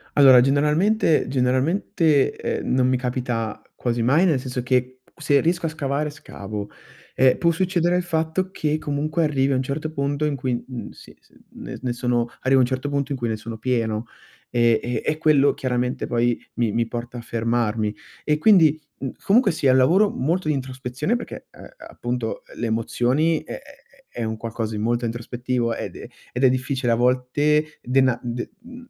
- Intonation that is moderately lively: Yes, average, 4.0 semitones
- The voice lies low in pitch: Yes, low, 130 Hz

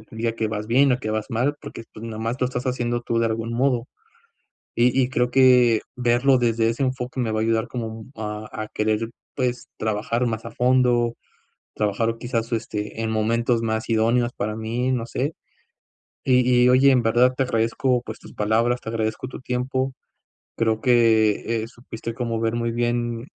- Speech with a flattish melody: Yes, narrow, 1.8 semitones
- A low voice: Yes, low, 115 Hz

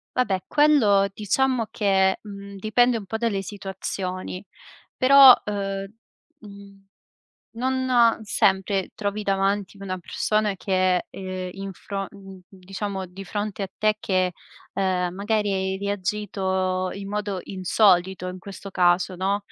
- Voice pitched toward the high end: Yes, high, 195 Hz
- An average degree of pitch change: No, narrow, 1.8 semitones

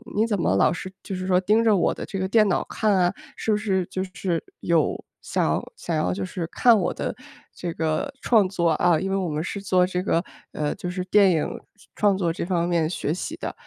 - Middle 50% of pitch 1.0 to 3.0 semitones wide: Yes, average, 2.7 semitones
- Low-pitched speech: No, medium, 185 Hz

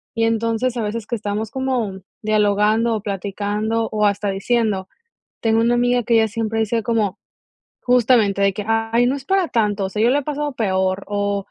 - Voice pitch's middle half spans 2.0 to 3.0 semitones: Yes, narrow, 2.4 semitones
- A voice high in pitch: Yes, high, 220 Hz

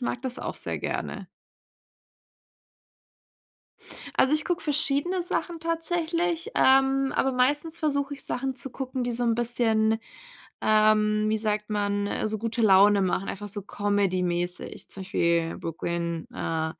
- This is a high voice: Yes, high, 230 Hz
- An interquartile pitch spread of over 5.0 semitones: Yes, wide, 5.6 semitones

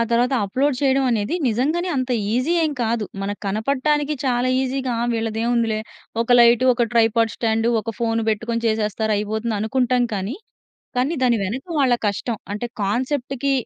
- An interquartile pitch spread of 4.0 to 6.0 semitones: No, average, 2.9 semitones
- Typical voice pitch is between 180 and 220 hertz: No, high, 235 Hz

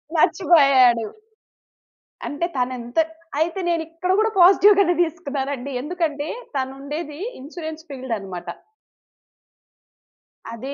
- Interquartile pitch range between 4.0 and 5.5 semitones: Yes, average, 4.5 semitones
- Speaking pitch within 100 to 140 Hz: No, very high, 295 Hz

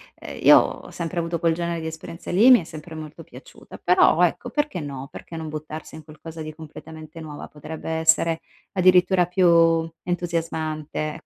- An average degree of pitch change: No, narrow, 1.8 semitones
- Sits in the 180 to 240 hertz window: No, medium, 165 Hz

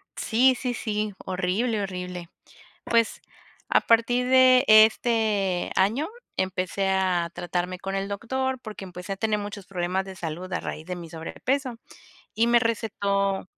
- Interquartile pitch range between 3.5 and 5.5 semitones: Yes, average, 4.0 semitones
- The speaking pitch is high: Yes, high, 200 Hz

